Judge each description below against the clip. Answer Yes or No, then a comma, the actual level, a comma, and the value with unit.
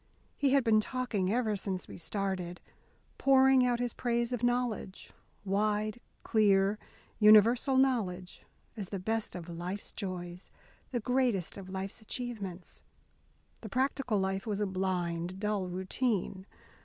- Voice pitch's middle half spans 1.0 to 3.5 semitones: No, average, 4.3 semitones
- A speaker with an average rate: No, slow, 130 wpm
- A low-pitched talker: No, high, 210 Hz